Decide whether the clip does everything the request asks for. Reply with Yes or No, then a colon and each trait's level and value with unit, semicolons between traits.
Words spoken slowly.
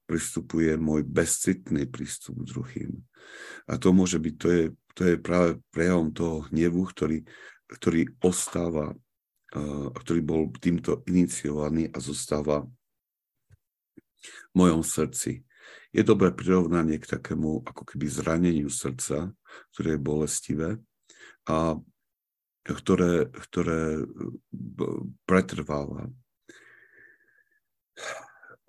Yes: slow, 95 wpm